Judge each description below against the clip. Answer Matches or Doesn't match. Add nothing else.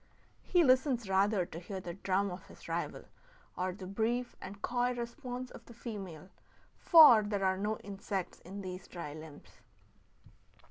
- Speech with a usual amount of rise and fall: Matches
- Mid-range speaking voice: Doesn't match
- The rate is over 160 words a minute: Doesn't match